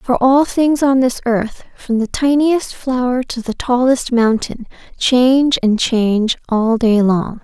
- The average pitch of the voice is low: No, high, 245 Hz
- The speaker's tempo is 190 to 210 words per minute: No, average, 160 wpm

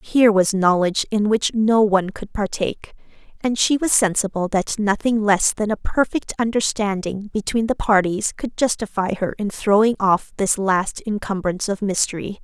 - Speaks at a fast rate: No, average, 165 wpm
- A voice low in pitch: No, high, 205 Hz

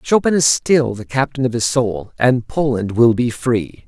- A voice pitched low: Yes, low, 125 Hz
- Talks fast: No, average, 185 wpm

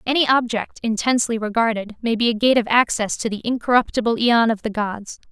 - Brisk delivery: No, average, 190 wpm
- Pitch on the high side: Yes, high, 225 Hz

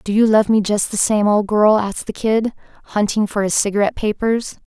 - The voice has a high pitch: Yes, high, 210 Hz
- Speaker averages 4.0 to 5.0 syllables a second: No, 5.5 syllables/s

